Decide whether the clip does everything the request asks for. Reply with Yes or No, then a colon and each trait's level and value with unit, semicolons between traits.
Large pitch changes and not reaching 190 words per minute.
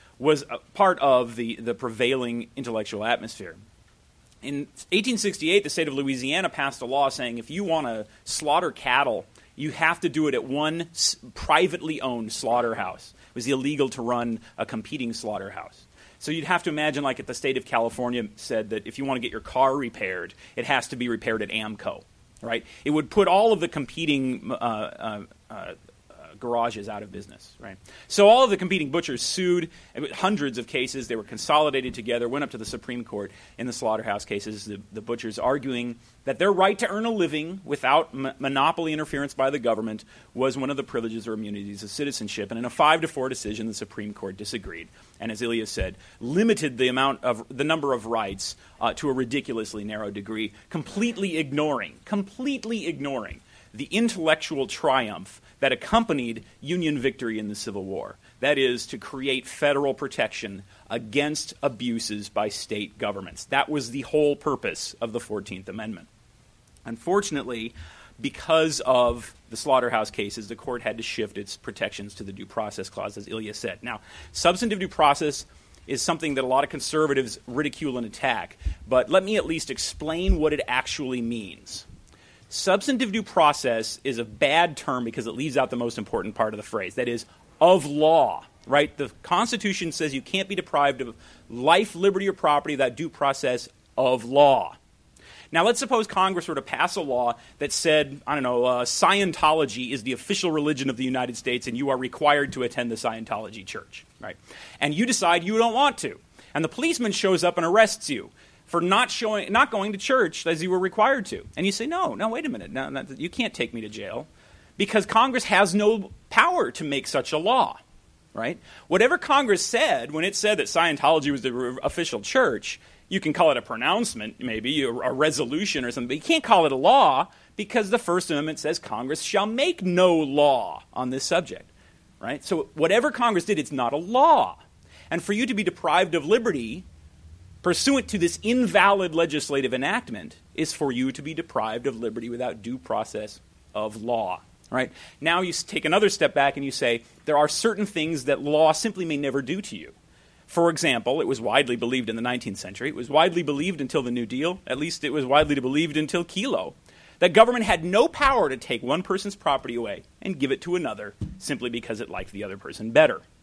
No: wide, 6.5 semitones; average, 195 wpm